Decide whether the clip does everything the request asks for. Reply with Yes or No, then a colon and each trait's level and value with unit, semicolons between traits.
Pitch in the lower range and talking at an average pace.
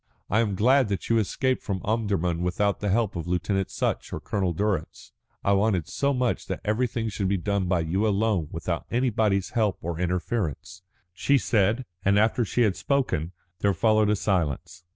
Yes: low, 100 Hz; average, 180 wpm